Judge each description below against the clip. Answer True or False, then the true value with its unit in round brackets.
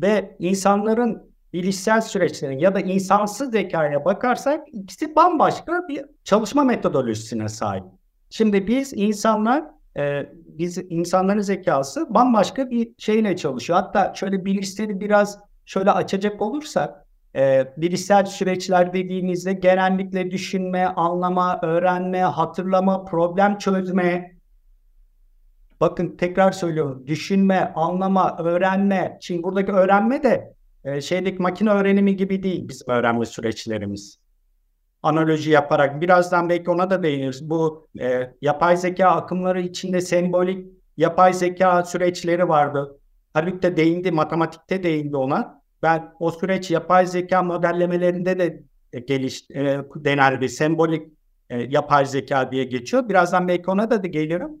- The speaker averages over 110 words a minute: True (120 wpm)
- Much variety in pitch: False (3.9 semitones)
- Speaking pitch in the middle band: True (180 Hz)